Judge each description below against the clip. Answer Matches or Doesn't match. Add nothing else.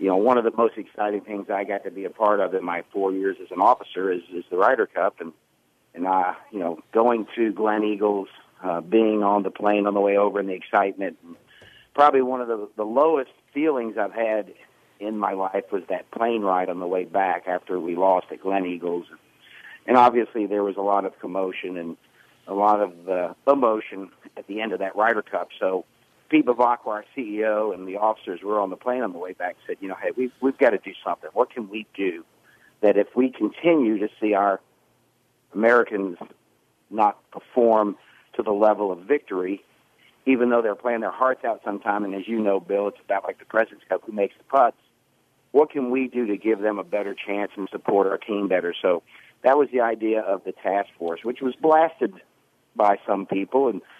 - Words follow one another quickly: Matches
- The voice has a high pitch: Doesn't match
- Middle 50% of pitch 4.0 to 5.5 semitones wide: Doesn't match